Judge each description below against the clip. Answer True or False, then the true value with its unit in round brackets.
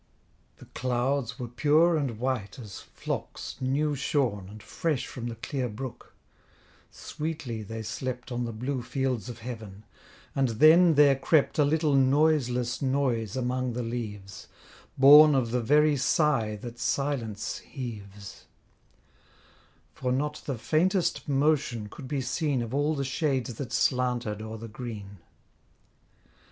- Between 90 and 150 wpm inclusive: True (140 wpm)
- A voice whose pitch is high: False (125 Hz)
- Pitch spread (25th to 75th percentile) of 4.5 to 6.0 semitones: False (3.8 semitones)